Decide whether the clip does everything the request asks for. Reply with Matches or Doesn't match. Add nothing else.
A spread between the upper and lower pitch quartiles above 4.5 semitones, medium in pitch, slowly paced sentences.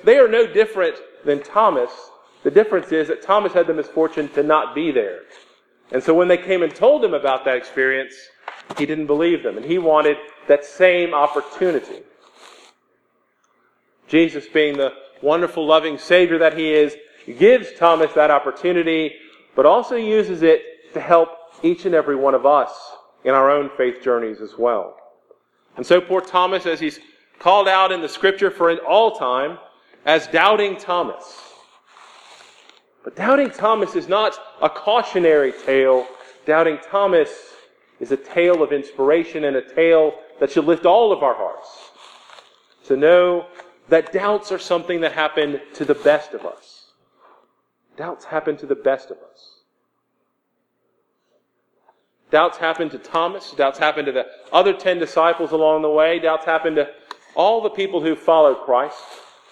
Doesn't match